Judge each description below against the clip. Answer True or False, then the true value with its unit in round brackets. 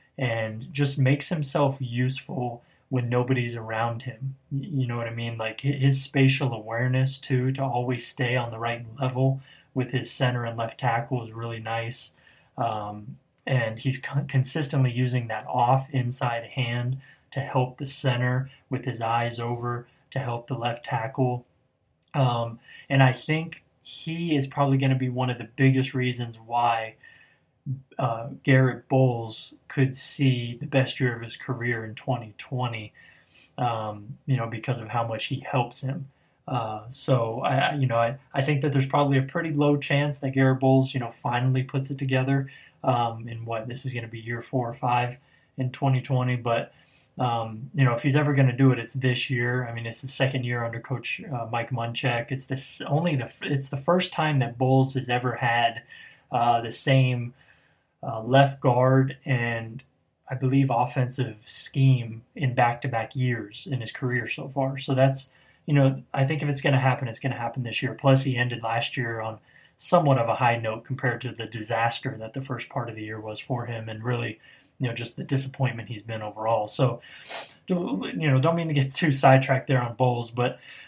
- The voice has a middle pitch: False (130 Hz)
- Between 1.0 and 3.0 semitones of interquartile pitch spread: True (2.4 semitones)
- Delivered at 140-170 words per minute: False (190 wpm)